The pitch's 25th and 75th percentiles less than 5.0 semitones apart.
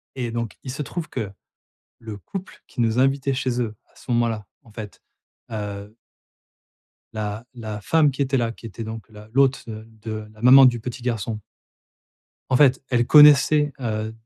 Yes: average, 3.6 semitones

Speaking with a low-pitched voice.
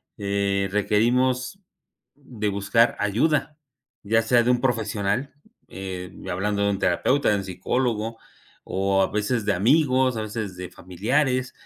Yes: low, 110 Hz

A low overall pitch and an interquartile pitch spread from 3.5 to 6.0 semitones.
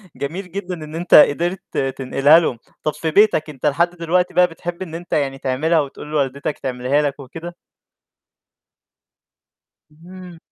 No: medium, 160 Hz; average, 3.8 semitones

